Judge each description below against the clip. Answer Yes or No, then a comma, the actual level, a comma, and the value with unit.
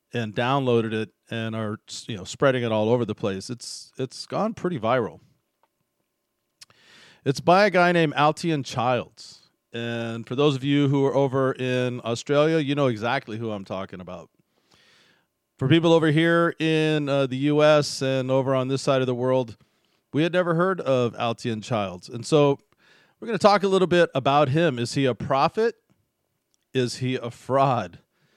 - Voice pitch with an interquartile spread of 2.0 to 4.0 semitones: No, average, 4.5 semitones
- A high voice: No, low, 135 Hz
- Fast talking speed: No, average, 180 wpm